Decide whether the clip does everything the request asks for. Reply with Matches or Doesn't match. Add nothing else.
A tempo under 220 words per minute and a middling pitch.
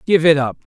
Doesn't match